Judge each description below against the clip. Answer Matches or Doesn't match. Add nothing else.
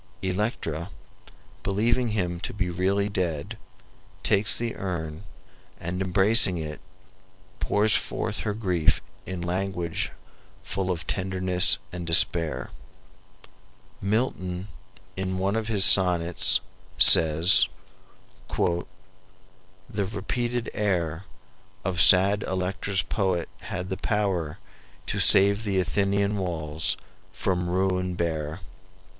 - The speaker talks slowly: Matches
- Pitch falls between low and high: Doesn't match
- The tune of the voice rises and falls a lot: Doesn't match